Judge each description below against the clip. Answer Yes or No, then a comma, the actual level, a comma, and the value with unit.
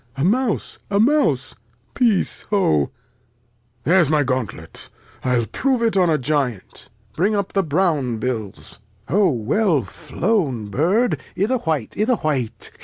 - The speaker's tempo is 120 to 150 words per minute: Yes, average, 140 wpm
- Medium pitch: Yes, medium, 155 Hz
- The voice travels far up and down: Yes, wide, 8.4 semitones